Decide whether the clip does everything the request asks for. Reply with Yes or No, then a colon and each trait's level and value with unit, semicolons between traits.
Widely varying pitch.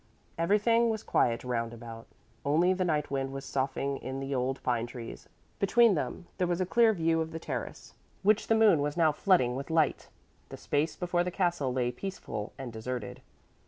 Yes: wide, 6.0 semitones